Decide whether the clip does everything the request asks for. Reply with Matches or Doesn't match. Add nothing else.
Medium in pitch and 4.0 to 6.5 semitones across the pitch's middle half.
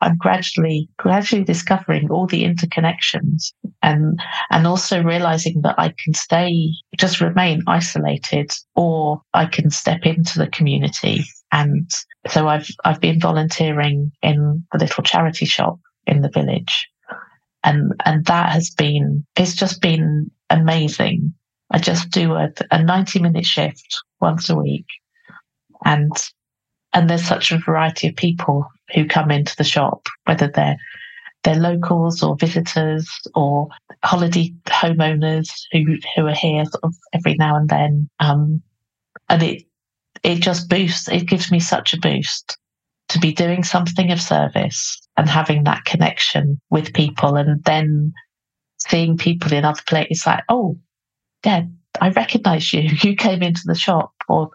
Doesn't match